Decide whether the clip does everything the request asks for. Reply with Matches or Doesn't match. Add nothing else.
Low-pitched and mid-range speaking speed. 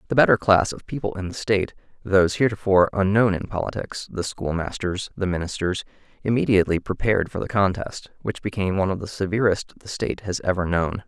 Matches